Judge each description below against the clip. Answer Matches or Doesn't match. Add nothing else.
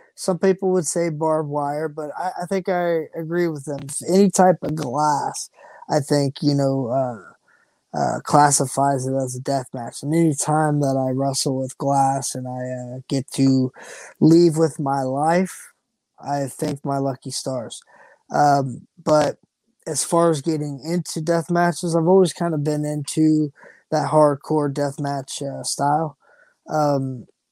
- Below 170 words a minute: Matches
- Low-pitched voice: Doesn't match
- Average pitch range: Matches